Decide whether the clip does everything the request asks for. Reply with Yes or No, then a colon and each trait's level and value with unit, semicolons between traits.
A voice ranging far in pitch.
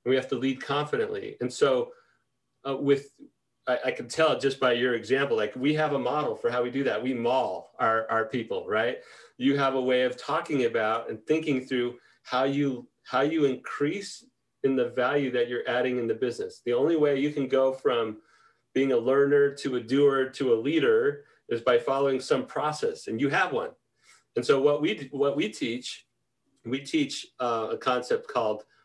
Yes: wide, 7.7 semitones